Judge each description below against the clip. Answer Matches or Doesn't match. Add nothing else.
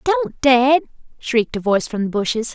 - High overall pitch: Matches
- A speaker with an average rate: Matches